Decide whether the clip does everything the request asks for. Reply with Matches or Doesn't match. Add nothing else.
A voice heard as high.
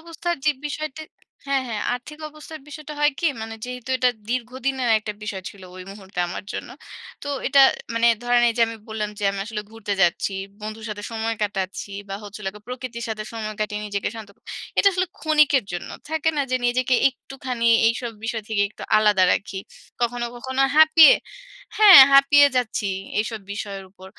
Matches